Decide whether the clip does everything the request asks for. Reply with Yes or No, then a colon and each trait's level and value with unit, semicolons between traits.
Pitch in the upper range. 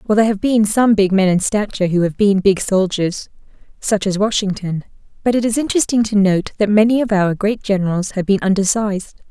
Yes: high, 200 Hz